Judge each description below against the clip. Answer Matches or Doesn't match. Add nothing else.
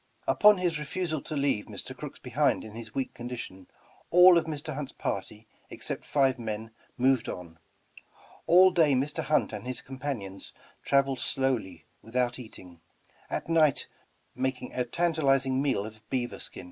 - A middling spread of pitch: Matches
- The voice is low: Matches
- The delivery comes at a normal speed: Matches